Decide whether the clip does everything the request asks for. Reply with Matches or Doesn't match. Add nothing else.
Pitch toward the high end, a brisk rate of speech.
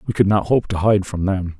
Doesn't match